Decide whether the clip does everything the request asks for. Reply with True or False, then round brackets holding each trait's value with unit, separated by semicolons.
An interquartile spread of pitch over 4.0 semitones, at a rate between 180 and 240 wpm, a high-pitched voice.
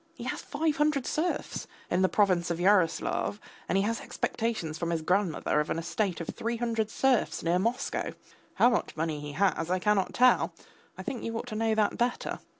True (5.2 semitones; 200 wpm; 205 Hz)